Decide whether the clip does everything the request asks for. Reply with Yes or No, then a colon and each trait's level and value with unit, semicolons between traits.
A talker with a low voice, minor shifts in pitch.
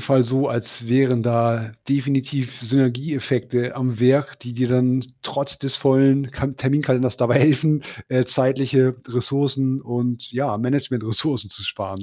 Yes: low, 130 Hz; narrow, 2.0 semitones